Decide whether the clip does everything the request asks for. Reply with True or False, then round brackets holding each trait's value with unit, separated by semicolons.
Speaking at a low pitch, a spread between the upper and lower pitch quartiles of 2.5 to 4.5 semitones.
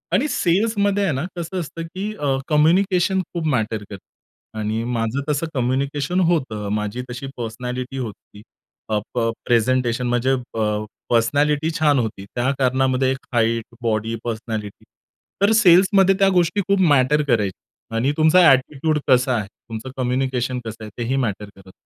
False (130 Hz; 5.6 semitones)